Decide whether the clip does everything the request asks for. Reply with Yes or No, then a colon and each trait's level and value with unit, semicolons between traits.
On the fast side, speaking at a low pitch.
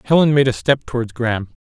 Yes: fast, 220 wpm; low, 125 Hz